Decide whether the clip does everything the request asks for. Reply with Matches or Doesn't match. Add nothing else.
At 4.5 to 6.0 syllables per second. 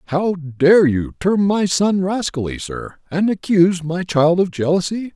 Doesn't match